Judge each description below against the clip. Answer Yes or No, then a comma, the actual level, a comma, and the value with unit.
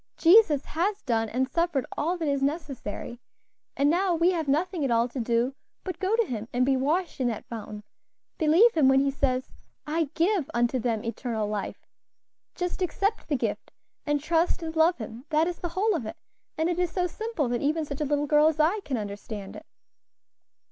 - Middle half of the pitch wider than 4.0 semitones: Yes, wide, 5.5 semitones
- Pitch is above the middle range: Yes, very high, 295 Hz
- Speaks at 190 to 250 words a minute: Yes, fast, 205 wpm